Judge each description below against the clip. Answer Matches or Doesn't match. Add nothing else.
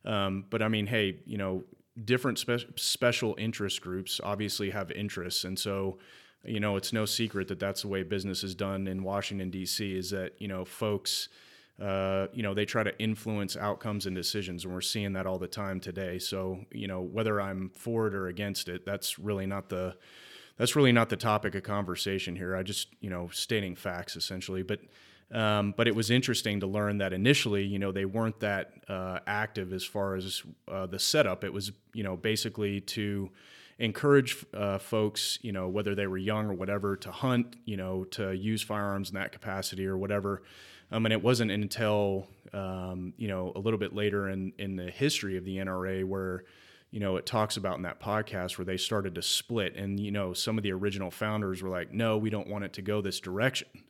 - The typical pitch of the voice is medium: Doesn't match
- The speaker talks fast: Matches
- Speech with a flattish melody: Matches